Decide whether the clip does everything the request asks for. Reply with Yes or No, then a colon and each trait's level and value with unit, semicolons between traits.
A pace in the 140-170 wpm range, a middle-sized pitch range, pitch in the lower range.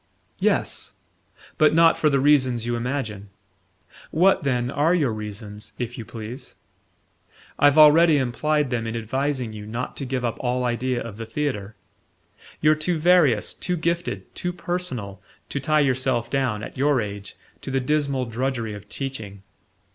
Yes: average, 155 wpm; average, 4.7 semitones; low, 130 Hz